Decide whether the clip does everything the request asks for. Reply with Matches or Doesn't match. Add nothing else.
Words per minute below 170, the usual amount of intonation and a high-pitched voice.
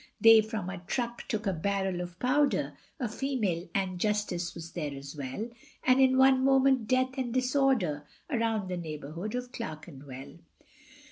Doesn't match